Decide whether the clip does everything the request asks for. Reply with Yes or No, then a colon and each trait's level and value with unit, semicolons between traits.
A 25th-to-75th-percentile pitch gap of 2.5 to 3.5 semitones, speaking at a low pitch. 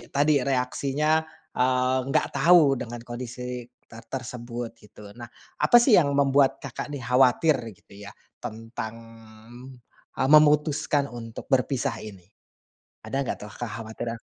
Yes: average, 3.2 semitones; low, 125 Hz